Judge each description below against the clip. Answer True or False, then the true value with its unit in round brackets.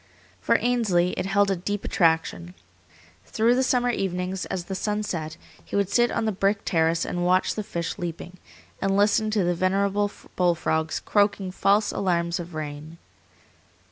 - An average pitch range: True (3.0 semitones)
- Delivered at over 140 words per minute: True (170 wpm)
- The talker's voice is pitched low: False (190 Hz)